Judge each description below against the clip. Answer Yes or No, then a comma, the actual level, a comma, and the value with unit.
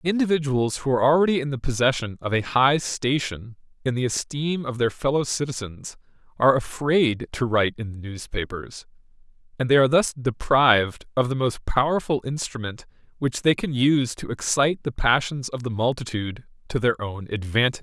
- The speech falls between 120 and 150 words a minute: No, average, 170 wpm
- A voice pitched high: No, low, 130 Hz